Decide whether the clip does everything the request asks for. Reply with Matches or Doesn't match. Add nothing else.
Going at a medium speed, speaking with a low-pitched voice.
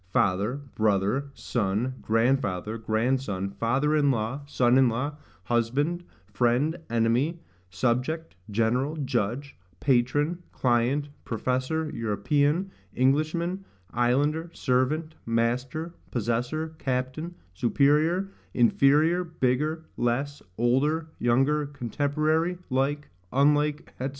Doesn't match